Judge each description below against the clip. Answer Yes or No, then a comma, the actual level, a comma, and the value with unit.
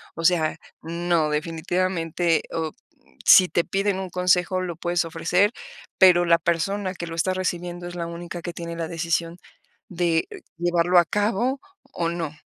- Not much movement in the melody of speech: Yes, narrow, 1.6 semitones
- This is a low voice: No, medium, 175 Hz